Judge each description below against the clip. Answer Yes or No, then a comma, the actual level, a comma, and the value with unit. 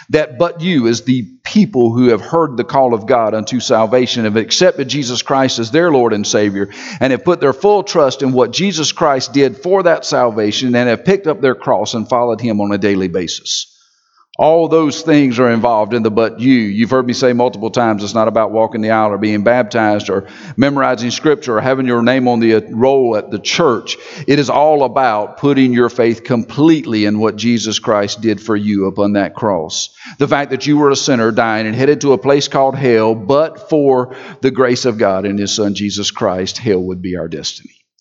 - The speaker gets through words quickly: Yes, fast, 215 wpm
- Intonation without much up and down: No, average, 4.1 semitones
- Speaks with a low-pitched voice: Yes, low, 120 Hz